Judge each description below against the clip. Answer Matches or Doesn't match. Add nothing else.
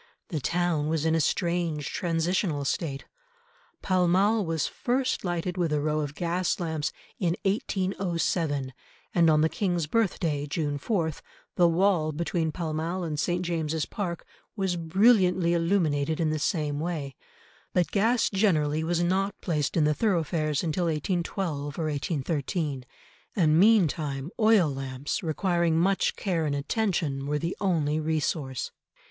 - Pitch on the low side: Doesn't match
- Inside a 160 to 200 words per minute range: Doesn't match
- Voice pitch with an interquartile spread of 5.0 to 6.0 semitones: Doesn't match